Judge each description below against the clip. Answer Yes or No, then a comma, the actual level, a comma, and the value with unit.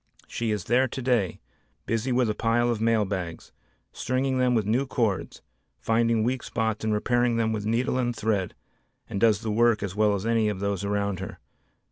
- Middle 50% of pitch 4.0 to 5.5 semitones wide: No, average, 2.7 semitones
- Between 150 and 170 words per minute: No, average, 190 wpm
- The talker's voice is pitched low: Yes, low, 110 Hz